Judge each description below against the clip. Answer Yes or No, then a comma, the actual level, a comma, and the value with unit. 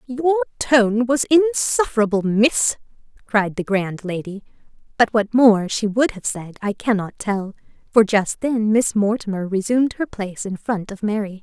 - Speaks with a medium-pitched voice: No, high, 220 Hz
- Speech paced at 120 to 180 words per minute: Yes, average, 170 wpm